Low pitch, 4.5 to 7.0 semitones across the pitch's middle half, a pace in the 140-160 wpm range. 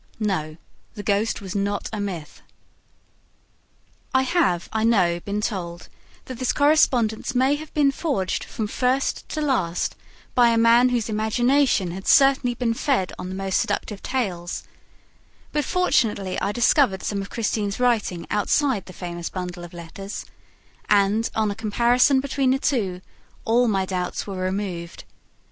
No: high, 215 Hz; average, 4.9 semitones; average, 150 wpm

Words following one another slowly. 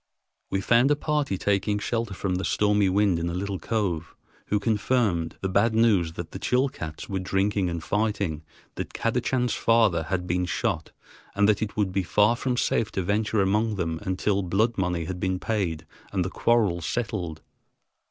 No: average, 180 wpm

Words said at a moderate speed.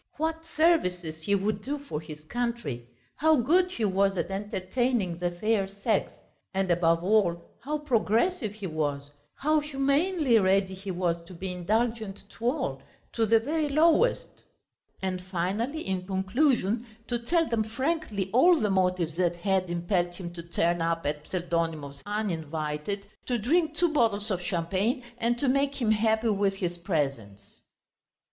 Yes: average, 155 wpm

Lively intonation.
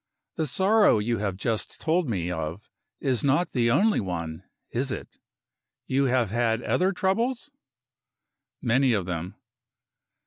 Yes: wide, 8.9 semitones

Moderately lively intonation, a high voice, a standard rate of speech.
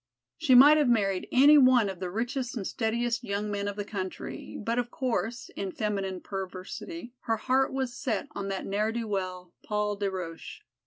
Yes: average, 3.9 semitones; high, 215 Hz; average, 190 wpm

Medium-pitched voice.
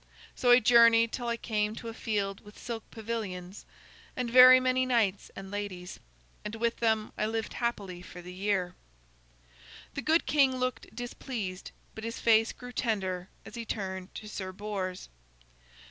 No: high, 220 Hz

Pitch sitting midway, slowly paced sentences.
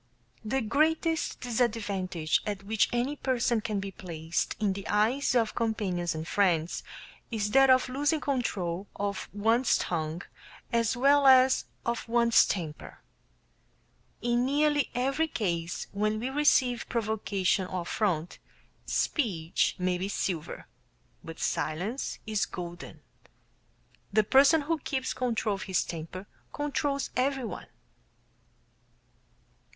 No: high, 220 Hz; slow, 120 wpm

